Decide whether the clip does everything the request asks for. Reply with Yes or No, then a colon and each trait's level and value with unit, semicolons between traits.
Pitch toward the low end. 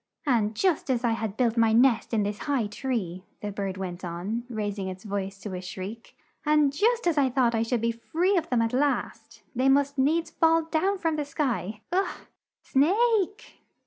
No: high, 240 Hz